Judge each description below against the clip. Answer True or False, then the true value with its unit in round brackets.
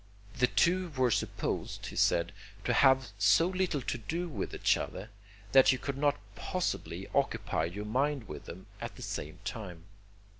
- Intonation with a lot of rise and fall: True (6.3 semitones)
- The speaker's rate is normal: True (165 wpm)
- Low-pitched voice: True (130 Hz)